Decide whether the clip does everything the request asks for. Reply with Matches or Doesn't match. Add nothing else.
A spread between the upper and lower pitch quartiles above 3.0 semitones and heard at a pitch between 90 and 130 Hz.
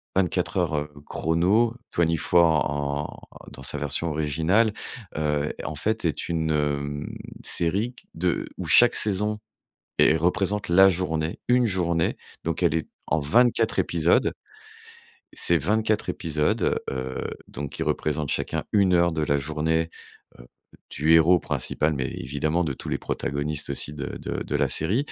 Doesn't match